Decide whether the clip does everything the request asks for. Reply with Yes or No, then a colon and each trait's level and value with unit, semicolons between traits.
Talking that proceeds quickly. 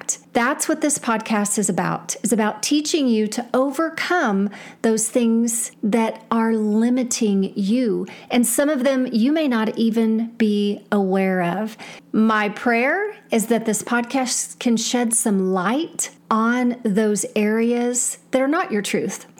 No: average, 145 wpm